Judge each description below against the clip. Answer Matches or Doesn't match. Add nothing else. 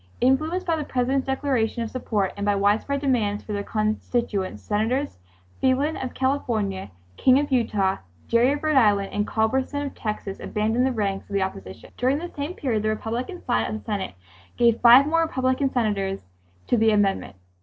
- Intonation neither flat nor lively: Matches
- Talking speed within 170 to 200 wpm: Matches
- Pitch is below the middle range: Doesn't match